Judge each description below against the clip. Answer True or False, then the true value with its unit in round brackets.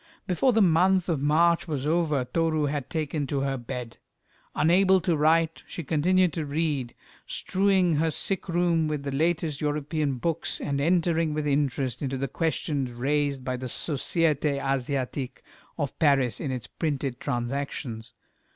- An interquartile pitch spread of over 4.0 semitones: False (3.4 semitones)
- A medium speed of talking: True (150 wpm)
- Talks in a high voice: False (150 Hz)